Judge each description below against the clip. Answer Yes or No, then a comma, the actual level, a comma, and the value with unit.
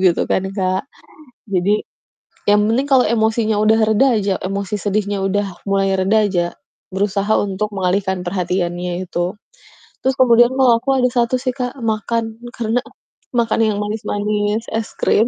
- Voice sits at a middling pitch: No, high, 210 Hz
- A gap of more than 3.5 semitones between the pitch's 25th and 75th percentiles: No, average, 3.0 semitones